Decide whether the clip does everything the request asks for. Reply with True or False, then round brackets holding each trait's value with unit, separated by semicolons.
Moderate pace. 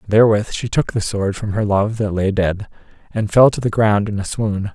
False (255 wpm)